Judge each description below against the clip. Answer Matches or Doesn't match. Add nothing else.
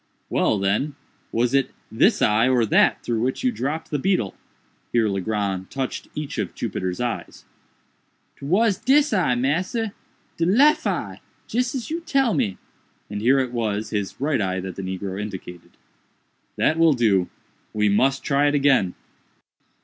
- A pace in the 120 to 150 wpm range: Matches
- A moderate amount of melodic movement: Doesn't match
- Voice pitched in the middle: Doesn't match